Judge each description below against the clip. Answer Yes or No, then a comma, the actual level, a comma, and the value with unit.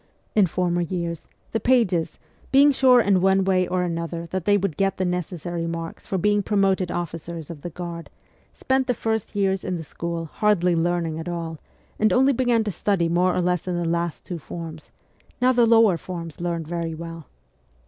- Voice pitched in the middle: Yes, medium, 175 Hz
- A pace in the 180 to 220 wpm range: Yes, average, 190 wpm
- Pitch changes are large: No, average, 3.1 semitones